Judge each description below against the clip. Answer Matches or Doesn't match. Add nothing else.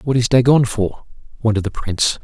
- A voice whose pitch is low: Matches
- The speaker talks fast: Doesn't match